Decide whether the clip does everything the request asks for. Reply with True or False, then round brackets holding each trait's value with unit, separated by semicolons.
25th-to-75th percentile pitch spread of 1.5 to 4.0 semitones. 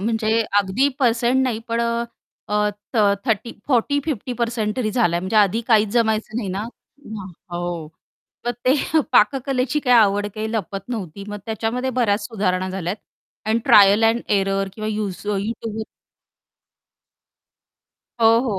True (2.9 semitones)